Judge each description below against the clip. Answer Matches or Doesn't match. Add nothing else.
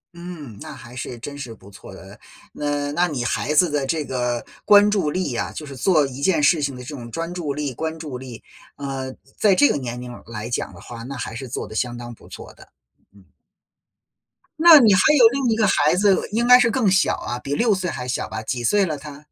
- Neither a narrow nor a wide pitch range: Doesn't match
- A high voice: Doesn't match